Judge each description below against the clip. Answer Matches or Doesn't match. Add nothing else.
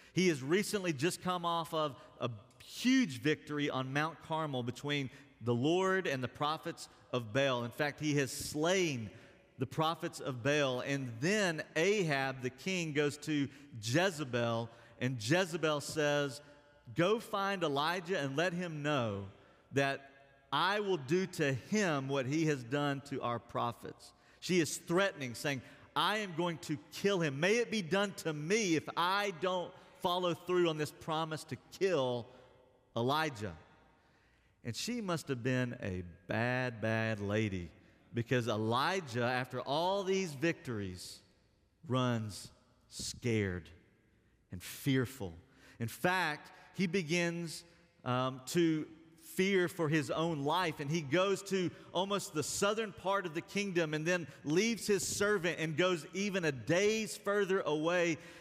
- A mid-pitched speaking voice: Matches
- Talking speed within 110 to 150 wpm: Matches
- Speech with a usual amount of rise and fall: Doesn't match